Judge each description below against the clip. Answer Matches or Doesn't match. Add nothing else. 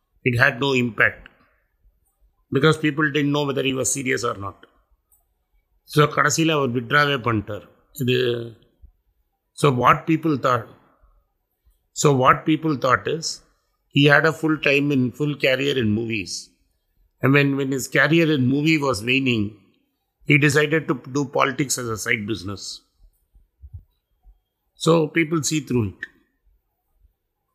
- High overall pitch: Doesn't match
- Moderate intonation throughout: Doesn't match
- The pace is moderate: Matches